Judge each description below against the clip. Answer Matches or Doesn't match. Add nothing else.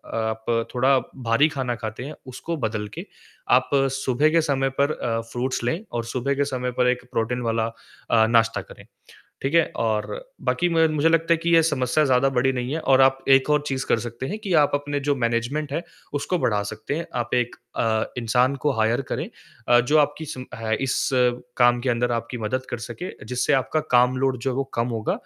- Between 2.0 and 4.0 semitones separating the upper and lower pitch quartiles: Matches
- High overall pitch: Doesn't match